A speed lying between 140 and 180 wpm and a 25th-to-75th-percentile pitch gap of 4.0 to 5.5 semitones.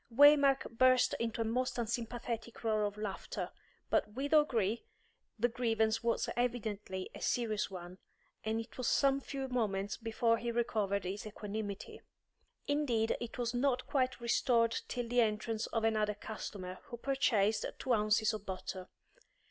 No: average, 150 wpm; narrow, 2.6 semitones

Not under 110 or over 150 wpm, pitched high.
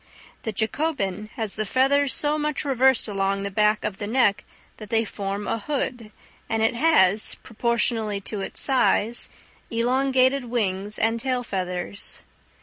Yes: average, 145 wpm; high, 225 Hz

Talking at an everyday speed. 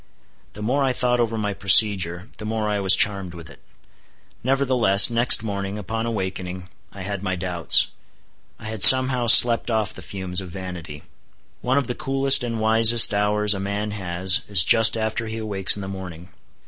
Yes: average, 175 wpm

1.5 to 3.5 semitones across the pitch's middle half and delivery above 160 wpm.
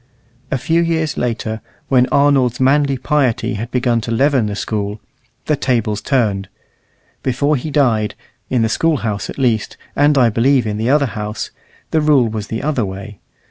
No: average, 4.4 semitones; average, 175 wpm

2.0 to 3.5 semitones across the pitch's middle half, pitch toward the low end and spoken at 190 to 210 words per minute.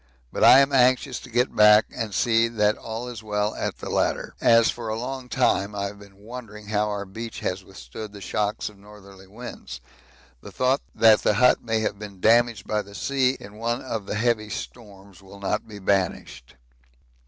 Yes: narrow, 2.6 semitones; low, 105 Hz; average, 200 wpm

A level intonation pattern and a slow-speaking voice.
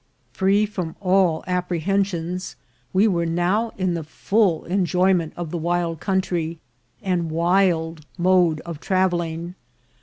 Yes: narrow, 2.2 semitones; slow, 125 wpm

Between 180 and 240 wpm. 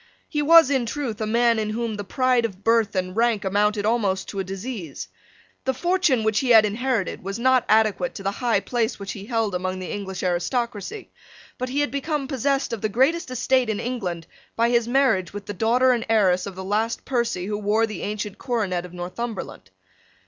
Yes: fast, 205 wpm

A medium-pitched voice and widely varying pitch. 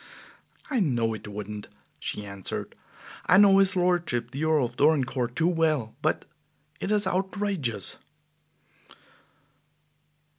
Yes: medium, 150 Hz; wide, 7.9 semitones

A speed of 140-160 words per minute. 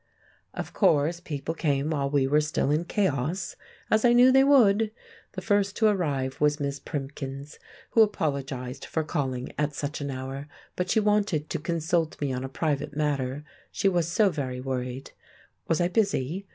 No: average, 175 wpm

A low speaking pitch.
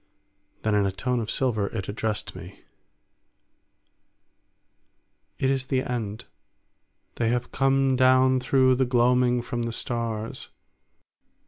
Yes: low, 120 Hz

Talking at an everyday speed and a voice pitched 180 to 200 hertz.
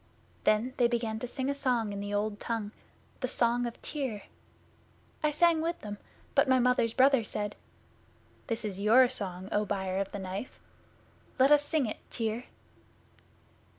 No: average, 165 wpm; high, 230 Hz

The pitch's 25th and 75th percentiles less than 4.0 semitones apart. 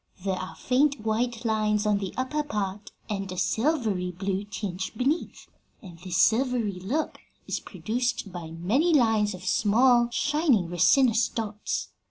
No: average, 4.7 semitones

